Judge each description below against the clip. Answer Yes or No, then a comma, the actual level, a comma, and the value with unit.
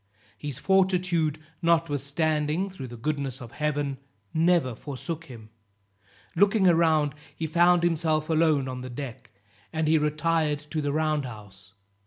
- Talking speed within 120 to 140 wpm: Yes, slow, 135 wpm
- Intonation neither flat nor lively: Yes, average, 3.2 semitones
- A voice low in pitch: No, medium, 155 Hz